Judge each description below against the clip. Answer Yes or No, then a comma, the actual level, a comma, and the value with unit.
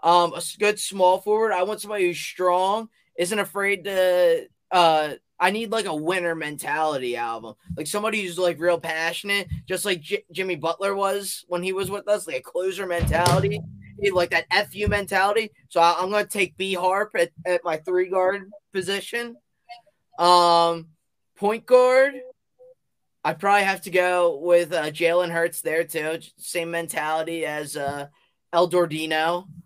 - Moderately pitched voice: Yes, medium, 180 Hz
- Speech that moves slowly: No, average, 160 wpm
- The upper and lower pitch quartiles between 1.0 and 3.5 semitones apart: Yes, average, 3.1 semitones